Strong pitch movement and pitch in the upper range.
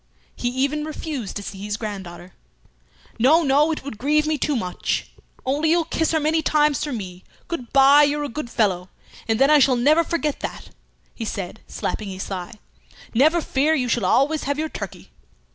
Yes: wide, 5.7 semitones; very high, 275 Hz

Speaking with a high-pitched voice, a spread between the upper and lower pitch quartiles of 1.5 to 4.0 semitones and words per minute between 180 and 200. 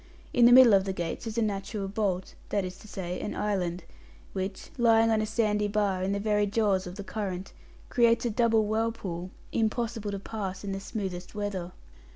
Yes: high, 205 Hz; narrow, 2.6 semitones; average, 195 wpm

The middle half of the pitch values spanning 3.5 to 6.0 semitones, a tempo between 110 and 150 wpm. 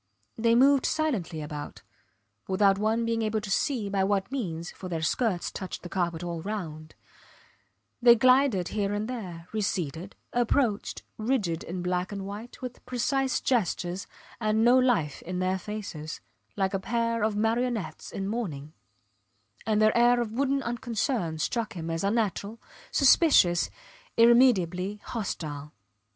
Yes: average, 4.9 semitones; average, 140 wpm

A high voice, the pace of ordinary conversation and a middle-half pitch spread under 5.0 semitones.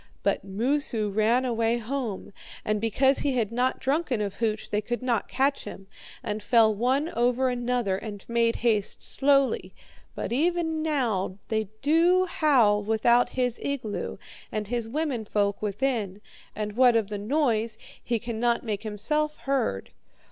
Yes: high, 235 Hz; average, 150 wpm; average, 4.0 semitones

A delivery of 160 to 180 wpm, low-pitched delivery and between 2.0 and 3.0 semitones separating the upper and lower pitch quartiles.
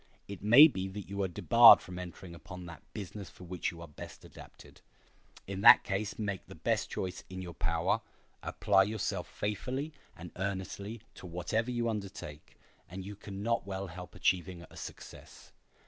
Yes: average, 175 wpm; very low, 95 Hz; narrow, 2.5 semitones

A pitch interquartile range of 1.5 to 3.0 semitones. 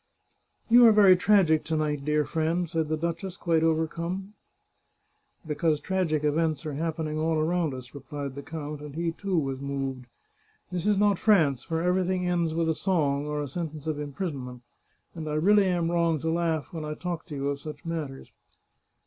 Yes: average, 2.7 semitones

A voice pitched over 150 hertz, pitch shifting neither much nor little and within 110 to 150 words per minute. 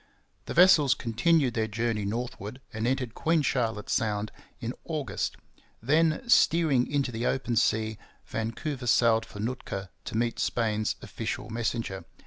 No: low, 120 Hz; average, 3.6 semitones; slow, 135 wpm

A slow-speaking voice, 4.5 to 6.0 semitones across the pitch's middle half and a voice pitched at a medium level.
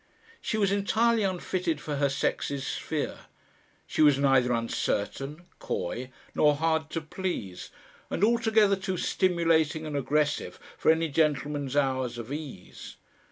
Yes: slow, 130 wpm; average, 4.8 semitones; medium, 155 Hz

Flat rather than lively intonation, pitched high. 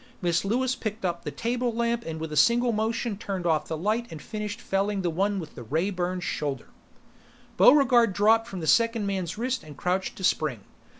No: average, 5.1 semitones; high, 200 Hz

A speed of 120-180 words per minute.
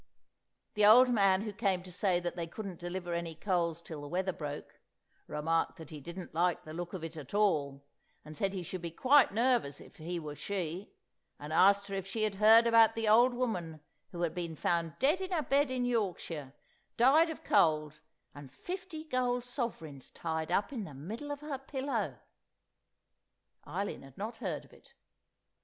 No: average, 190 wpm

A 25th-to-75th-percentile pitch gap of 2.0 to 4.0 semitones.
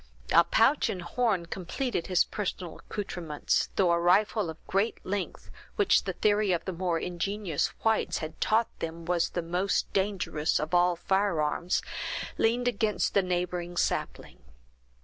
Yes: average, 3.3 semitones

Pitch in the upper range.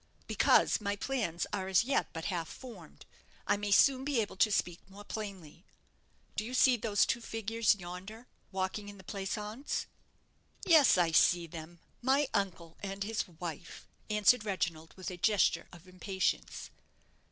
Yes: high, 200 Hz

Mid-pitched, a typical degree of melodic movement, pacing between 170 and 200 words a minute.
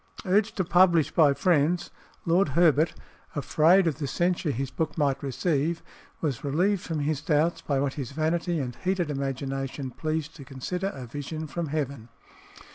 No: medium, 155 Hz; average, 3.7 semitones; average, 160 wpm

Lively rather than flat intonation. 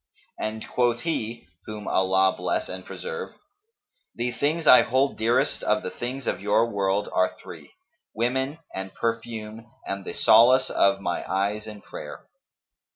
No: average, 3.9 semitones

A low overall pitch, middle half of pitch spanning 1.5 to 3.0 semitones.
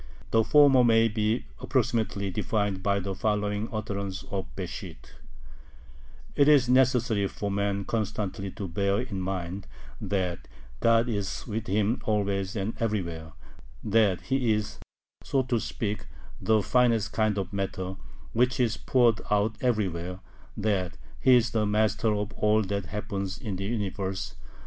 Yes: low, 105 Hz; narrow, 2.6 semitones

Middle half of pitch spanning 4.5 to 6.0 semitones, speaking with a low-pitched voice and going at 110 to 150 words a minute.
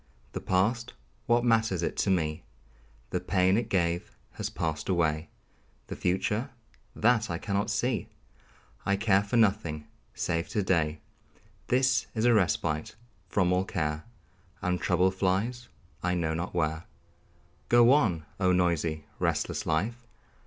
Yes: average, 5.0 semitones; very low, 95 Hz; average, 140 wpm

